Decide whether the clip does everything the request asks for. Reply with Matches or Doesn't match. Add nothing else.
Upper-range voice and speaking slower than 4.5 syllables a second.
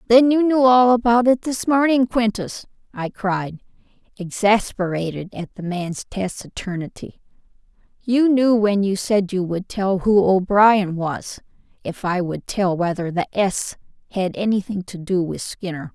Matches